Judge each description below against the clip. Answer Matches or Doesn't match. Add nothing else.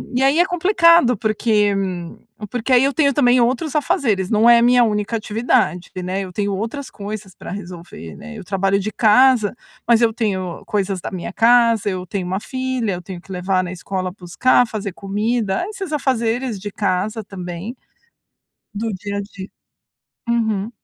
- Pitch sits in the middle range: Doesn't match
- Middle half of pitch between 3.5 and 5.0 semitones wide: Matches